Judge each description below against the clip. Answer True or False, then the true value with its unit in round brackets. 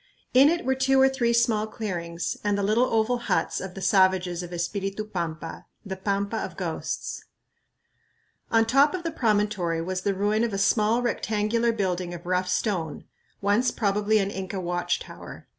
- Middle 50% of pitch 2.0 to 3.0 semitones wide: False (3.8 semitones)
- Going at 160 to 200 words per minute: True (175 wpm)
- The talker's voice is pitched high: True (205 Hz)